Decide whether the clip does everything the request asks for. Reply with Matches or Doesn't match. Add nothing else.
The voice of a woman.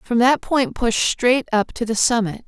Matches